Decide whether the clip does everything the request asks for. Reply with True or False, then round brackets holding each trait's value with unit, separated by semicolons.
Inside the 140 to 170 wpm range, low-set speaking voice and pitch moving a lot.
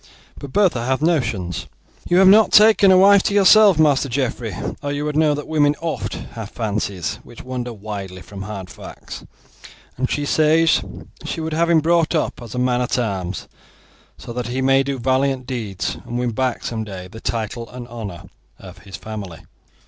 False (185 wpm; 125 Hz; 6.0 semitones)